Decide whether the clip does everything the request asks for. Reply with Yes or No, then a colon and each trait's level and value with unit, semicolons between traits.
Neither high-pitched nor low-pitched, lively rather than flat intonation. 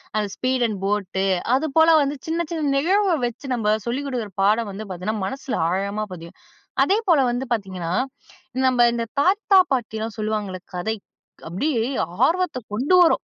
No: high, 235 Hz; wide, 5.9 semitones